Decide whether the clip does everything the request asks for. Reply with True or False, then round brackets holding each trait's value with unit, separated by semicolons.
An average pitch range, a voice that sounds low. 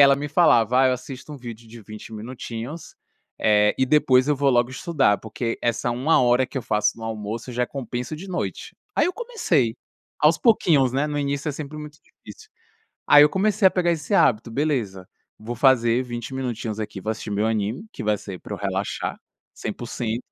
True (4.6 semitones; 125 Hz)